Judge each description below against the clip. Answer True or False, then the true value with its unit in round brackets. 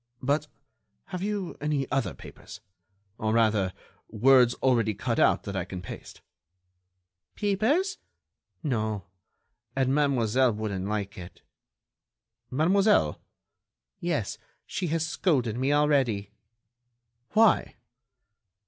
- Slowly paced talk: True (100 wpm)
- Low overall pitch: True (130 Hz)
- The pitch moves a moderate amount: False (6.2 semitones)